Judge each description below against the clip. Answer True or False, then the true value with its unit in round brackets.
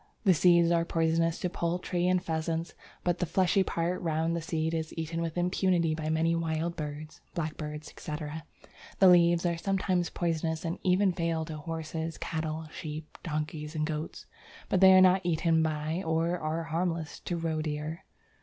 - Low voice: False (165 Hz)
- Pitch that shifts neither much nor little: False (1.7 semitones)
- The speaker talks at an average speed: True (165 wpm)